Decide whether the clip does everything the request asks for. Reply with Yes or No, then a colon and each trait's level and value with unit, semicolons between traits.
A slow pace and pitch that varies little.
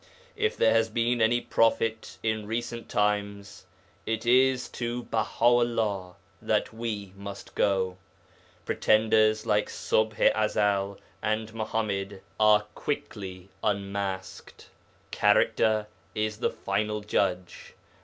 Yes: slow, 110 wpm; narrow, 2.0 semitones